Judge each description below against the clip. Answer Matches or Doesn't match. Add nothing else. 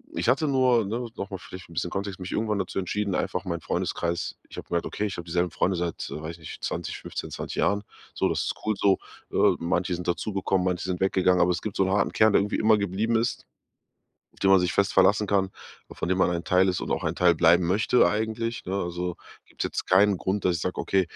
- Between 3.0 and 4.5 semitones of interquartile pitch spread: Doesn't match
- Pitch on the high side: Doesn't match